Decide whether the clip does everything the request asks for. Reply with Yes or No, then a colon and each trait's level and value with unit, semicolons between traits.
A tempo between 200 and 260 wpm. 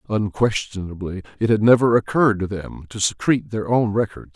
No: average, 165 wpm